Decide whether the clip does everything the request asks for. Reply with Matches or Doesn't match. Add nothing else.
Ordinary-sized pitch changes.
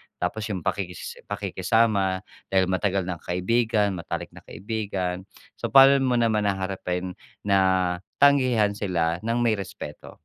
Matches